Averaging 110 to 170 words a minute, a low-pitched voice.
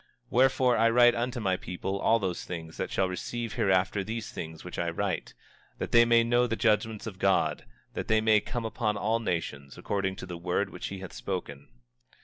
No: average, 200 wpm; low, 105 Hz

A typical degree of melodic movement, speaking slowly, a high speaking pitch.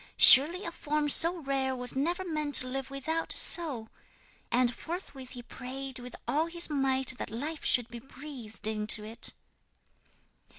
No: average, 3.8 semitones; average, 160 wpm; very high, 270 Hz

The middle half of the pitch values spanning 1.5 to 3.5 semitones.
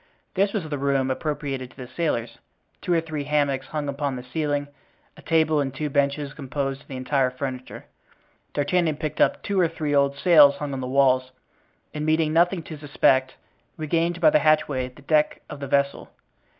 Yes: narrow, 2.5 semitones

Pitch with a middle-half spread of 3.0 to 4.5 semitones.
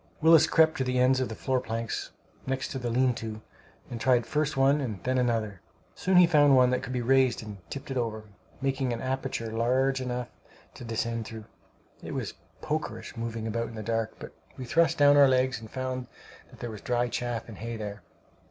No: narrow, 2.6 semitones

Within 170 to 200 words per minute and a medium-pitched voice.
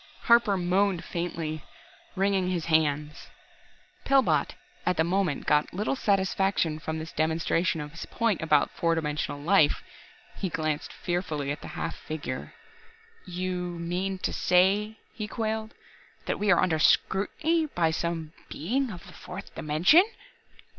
No: average, 140 wpm; medium, 175 Hz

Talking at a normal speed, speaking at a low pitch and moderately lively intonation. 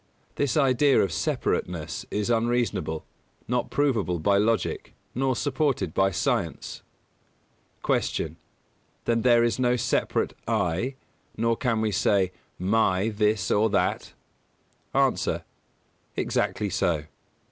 No: slow, 115 wpm; low, 110 Hz; average, 4.3 semitones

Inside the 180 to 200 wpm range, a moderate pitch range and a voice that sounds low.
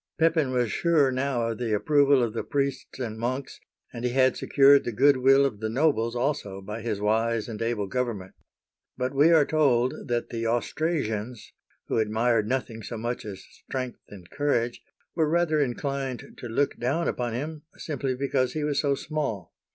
Yes: average, 185 wpm; average, 3.6 semitones; low, 125 Hz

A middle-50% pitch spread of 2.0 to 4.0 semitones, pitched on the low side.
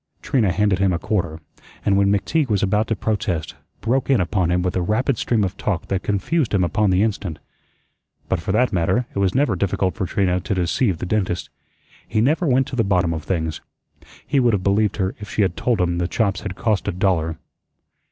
Yes: average, 3.3 semitones; low, 100 Hz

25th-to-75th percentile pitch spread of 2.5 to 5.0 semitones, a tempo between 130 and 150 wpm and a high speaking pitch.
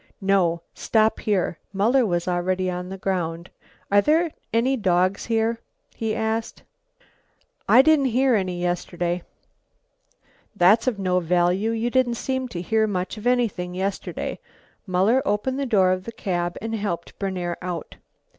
Yes: average, 4.1 semitones; average, 145 wpm; high, 195 Hz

